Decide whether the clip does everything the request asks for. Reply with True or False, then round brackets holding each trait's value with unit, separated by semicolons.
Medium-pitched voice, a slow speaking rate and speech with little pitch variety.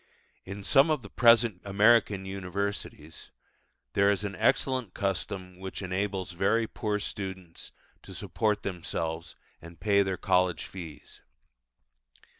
False (100 Hz; 120 wpm; 2.2 semitones)